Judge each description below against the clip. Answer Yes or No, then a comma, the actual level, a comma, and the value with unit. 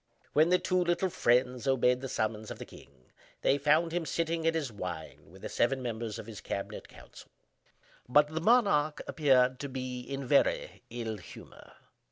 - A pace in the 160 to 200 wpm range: Yes, average, 185 wpm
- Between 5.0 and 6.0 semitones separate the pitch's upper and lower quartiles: Yes, average, 5.3 semitones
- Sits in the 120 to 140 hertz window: Yes, low, 135 Hz